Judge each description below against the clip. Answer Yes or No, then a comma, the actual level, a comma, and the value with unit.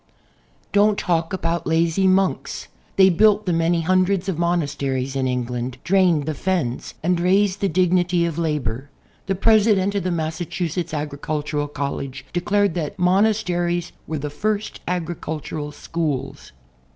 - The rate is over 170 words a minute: No, average, 140 wpm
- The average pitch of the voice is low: No, medium, 170 Hz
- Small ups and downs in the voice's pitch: No, average, 4.0 semitones